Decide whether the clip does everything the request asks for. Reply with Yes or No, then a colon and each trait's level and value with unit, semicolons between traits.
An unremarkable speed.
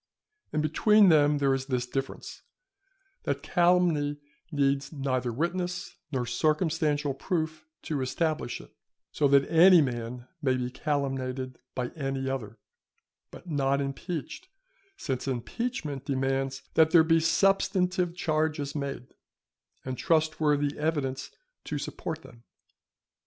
No: slow, 120 wpm